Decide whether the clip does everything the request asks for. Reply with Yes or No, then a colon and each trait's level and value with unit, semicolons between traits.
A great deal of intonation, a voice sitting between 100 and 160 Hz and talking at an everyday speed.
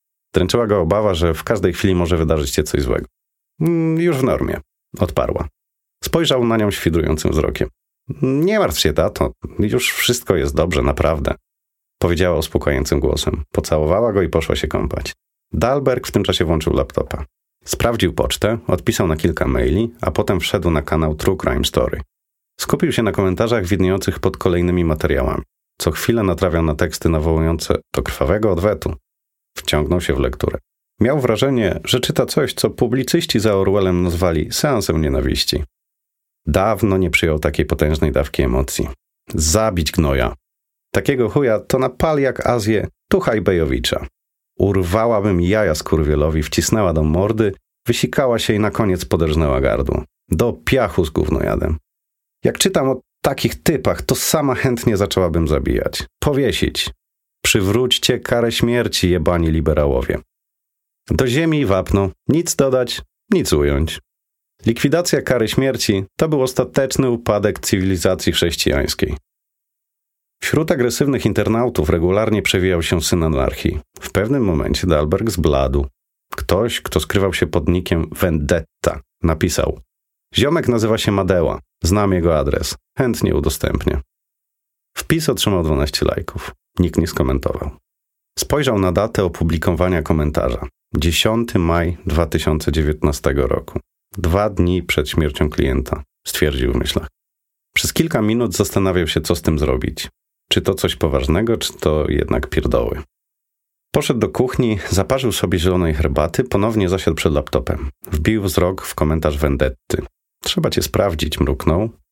No: wide, 5.8 semitones; very low, 90 Hz; average, 135 wpm